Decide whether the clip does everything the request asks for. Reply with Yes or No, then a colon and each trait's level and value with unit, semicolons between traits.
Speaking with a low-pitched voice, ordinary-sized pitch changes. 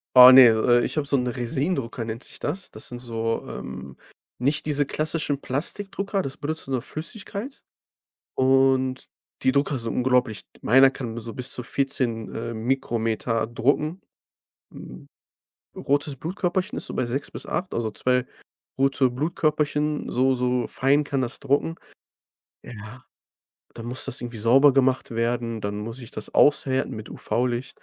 Yes: low, 130 Hz; average, 3.4 semitones